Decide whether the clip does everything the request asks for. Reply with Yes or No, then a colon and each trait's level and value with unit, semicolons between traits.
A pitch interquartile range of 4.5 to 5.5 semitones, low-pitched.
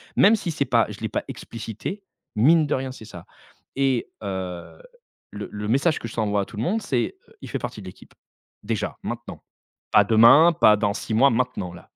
Yes: average, 4.8 semitones; low, 115 Hz